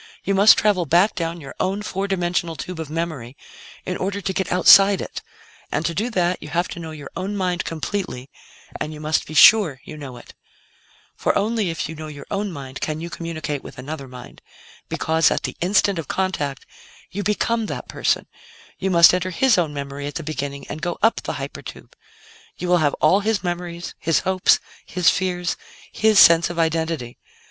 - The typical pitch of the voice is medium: Yes, medium, 170 Hz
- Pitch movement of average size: Yes, average, 3.7 semitones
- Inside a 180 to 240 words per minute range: Yes, average, 200 wpm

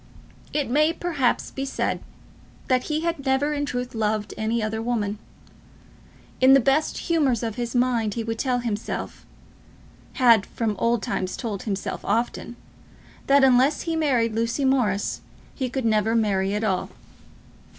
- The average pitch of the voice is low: No, high, 240 Hz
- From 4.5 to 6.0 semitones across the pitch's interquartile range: No, average, 3.7 semitones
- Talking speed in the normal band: Yes, average, 150 wpm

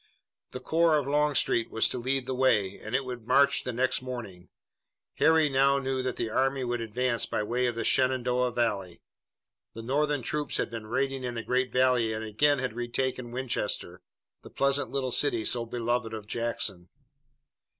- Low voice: Yes, low, 125 Hz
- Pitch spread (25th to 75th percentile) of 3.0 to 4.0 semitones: No, narrow, 2.5 semitones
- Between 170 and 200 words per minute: Yes, average, 180 wpm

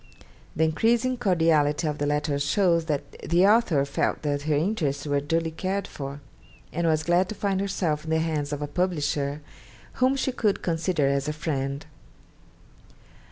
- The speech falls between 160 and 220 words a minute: Yes, average, 165 wpm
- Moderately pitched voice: Yes, medium, 160 Hz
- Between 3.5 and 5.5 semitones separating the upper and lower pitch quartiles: Yes, average, 4.2 semitones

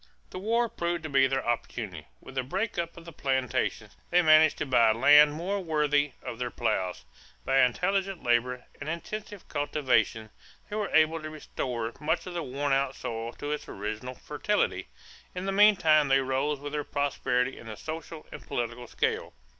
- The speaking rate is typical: Yes, average, 180 wpm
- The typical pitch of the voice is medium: Yes, medium, 145 Hz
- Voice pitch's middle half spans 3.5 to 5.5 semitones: Yes, average, 4.9 semitones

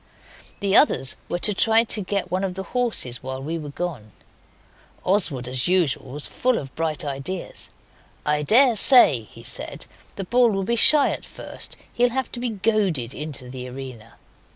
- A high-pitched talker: No, medium, 180 Hz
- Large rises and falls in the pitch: Yes, wide, 8.6 semitones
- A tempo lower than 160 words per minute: No, average, 175 wpm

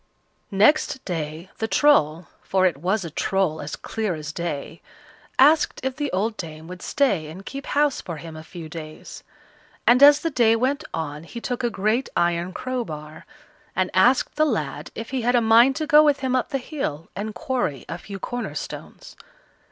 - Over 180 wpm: Yes, average, 190 wpm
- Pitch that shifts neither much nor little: No, wide, 8.0 semitones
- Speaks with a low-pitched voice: No, high, 205 Hz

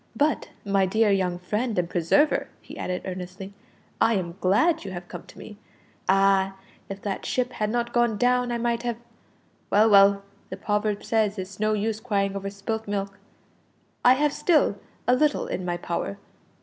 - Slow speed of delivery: No, average, 180 wpm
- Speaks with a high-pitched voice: Yes, high, 205 Hz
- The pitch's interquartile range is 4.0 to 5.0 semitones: No, average, 3.5 semitones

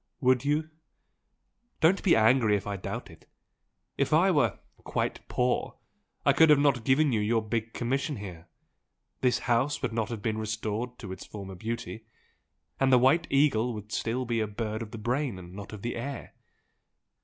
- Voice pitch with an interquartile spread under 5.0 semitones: Yes, average, 3.6 semitones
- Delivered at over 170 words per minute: Yes, average, 180 wpm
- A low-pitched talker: Yes, low, 115 Hz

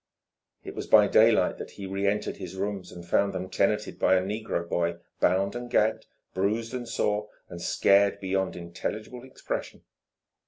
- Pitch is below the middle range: Yes, low, 100 Hz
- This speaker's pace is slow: No, average, 160 wpm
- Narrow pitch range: Yes, narrow, 2.3 semitones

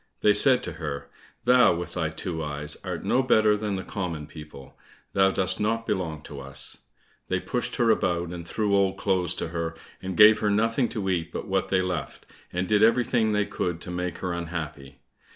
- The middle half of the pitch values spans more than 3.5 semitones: Yes, average, 4.2 semitones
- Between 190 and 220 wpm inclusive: Yes, fast, 205 wpm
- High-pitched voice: No, very low, 90 Hz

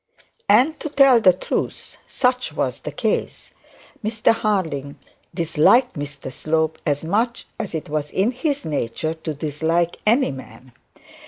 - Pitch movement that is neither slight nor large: No, wide, 7.8 semitones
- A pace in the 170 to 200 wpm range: No, average, 140 wpm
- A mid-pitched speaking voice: Yes, medium, 165 Hz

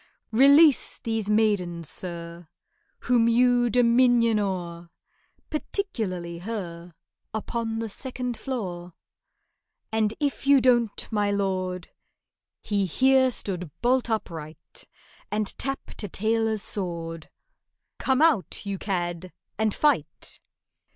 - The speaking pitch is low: No, high, 215 Hz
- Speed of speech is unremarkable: No, slow, 105 wpm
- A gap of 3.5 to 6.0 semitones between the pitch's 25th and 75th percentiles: Yes, average, 5.3 semitones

